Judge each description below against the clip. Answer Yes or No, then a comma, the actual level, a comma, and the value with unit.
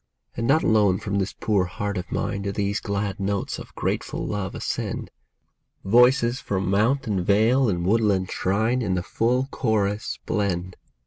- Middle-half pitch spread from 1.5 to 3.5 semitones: Yes, average, 2.9 semitones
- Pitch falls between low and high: No, low, 100 Hz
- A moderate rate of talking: Yes, average, 165 wpm